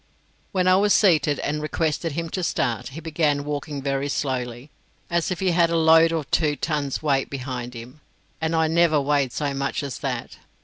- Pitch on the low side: No, medium, 150 Hz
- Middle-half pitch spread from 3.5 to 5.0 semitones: No, average, 3.1 semitones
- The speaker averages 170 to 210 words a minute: Yes, average, 190 wpm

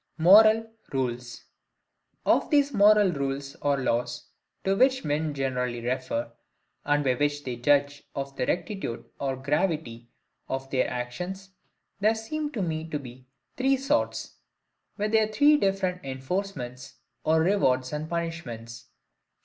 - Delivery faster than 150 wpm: No, slow, 135 wpm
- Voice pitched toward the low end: No, medium, 145 Hz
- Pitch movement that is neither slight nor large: No, wide, 7.3 semitones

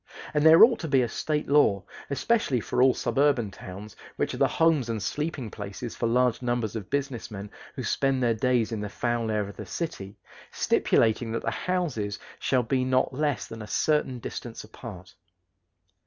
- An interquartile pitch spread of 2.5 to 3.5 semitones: No, average, 4.4 semitones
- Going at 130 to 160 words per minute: No, average, 185 wpm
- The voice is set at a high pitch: No, low, 120 Hz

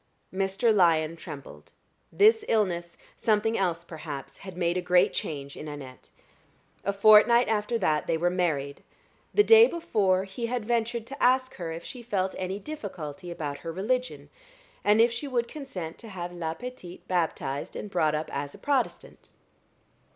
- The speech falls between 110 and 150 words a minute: No, average, 165 wpm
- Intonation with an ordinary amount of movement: No, wide, 6.1 semitones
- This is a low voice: No, high, 190 Hz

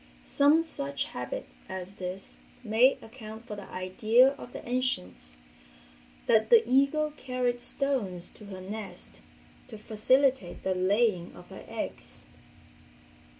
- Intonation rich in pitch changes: Yes, wide, 5.7 semitones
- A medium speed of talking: No, slow, 125 wpm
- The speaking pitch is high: Yes, high, 220 Hz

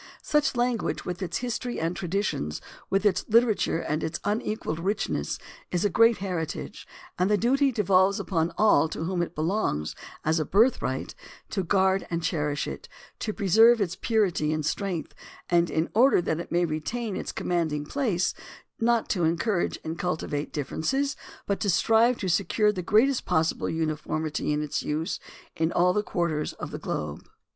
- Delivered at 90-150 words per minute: No, average, 170 wpm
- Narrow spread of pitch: No, average, 5.0 semitones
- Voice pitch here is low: No, medium, 180 Hz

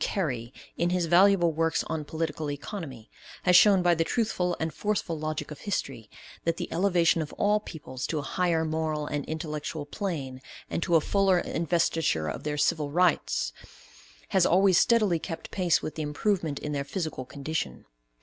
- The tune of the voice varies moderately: Yes, average, 3.4 semitones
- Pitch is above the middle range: No, medium, 160 Hz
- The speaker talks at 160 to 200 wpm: Yes, average, 170 wpm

